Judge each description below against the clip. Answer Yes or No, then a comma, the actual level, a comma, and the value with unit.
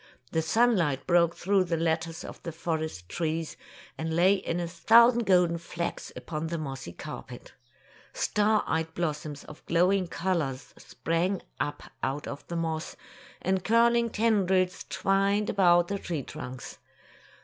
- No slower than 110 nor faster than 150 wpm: Yes, average, 145 wpm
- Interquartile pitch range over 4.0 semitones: No, average, 3.3 semitones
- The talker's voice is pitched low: No, medium, 170 Hz